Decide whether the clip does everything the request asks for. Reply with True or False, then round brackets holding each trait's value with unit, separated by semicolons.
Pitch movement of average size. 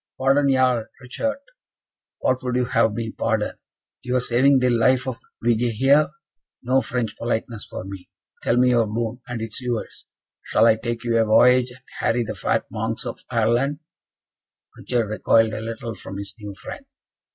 False (2.1 semitones)